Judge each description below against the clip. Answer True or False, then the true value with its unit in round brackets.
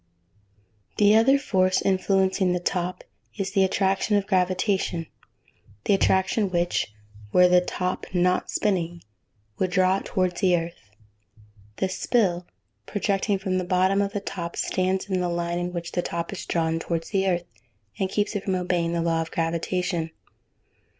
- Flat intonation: True (2.0 semitones)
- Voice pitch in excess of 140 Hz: True (185 Hz)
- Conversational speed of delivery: True (160 wpm)